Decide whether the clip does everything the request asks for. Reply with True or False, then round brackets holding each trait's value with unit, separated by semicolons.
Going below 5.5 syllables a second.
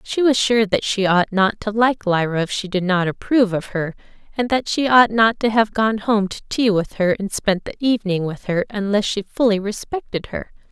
True (5.0 syllables/s)